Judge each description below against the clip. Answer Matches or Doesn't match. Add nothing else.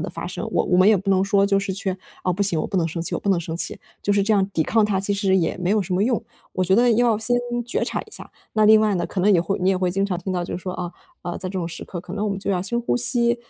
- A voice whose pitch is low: Doesn't match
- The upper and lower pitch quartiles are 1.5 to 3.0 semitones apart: Matches